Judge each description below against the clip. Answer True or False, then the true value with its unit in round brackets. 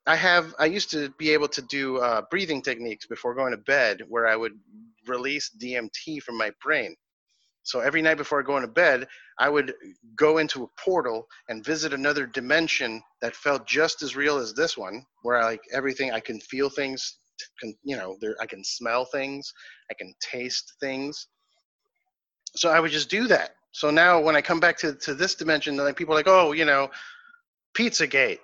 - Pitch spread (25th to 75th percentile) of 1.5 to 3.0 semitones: False (3.7 semitones)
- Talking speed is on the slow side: False (195 wpm)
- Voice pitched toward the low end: False (145 Hz)